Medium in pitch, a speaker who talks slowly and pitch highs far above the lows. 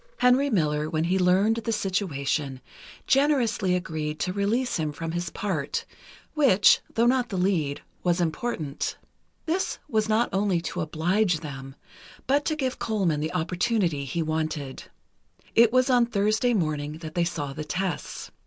No: medium, 180 Hz; average, 155 wpm; wide, 6.3 semitones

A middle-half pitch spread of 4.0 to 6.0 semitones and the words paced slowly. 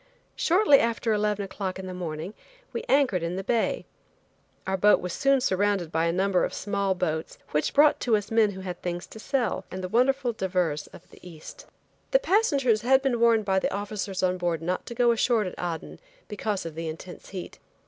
No: average, 4.5 semitones; fast, 205 wpm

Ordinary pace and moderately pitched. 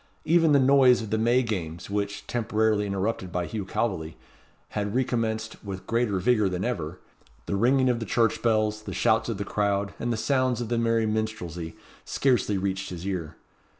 No: average, 185 wpm; low, 110 Hz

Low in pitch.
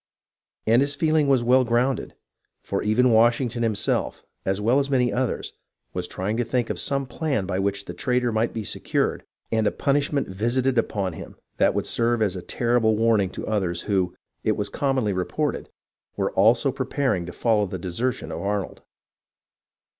Yes: low, 115 Hz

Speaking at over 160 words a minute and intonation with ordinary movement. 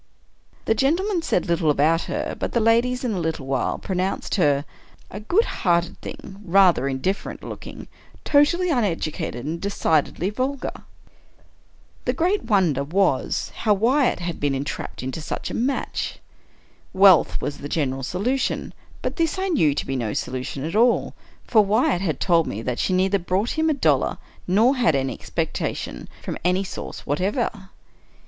No: average, 170 wpm; wide, 7.6 semitones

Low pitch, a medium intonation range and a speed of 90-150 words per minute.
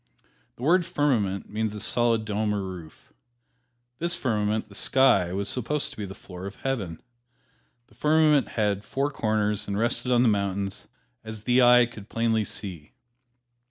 No: low, 110 Hz; average, 3.8 semitones; average, 160 wpm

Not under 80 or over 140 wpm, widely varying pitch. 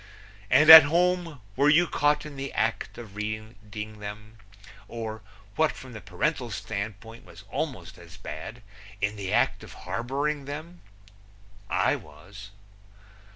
Yes: slow, 135 wpm; wide, 5.7 semitones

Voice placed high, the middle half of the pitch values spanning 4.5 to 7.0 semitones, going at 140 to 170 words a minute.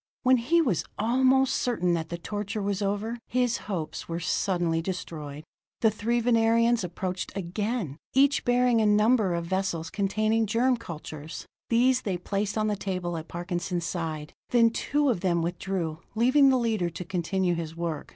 Yes: high, 200 Hz; average, 5.2 semitones; average, 165 wpm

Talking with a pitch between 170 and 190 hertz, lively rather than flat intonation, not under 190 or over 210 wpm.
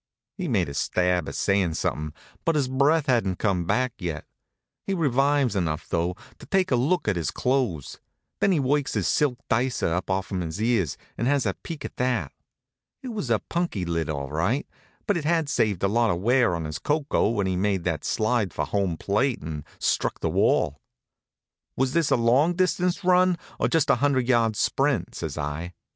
No: low, 115 Hz; wide, 8.2 semitones; average, 195 wpm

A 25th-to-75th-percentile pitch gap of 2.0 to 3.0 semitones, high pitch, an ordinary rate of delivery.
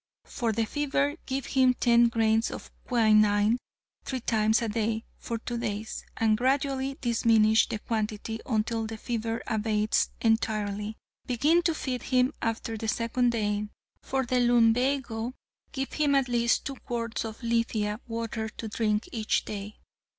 Yes: narrow, 2.4 semitones; high, 230 Hz; average, 150 wpm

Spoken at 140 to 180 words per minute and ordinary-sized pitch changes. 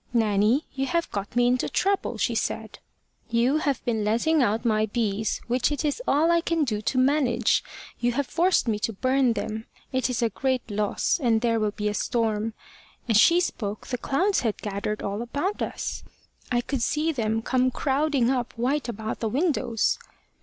No: average, 190 wpm; average, 4.1 semitones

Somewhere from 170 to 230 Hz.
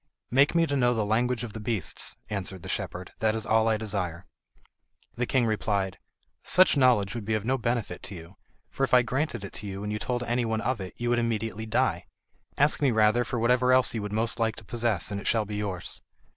No: low, 110 Hz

